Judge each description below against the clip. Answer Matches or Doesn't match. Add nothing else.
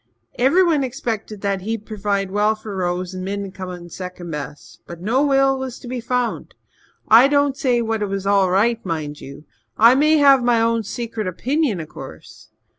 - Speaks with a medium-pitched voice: Doesn't match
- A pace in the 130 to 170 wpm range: Doesn't match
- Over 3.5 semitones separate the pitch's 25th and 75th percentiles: Matches